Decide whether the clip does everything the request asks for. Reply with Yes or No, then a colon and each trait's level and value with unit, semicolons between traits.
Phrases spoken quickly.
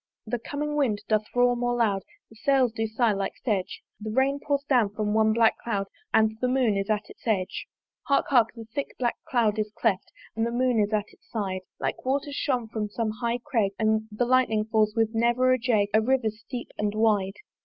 Yes: fast, 210 wpm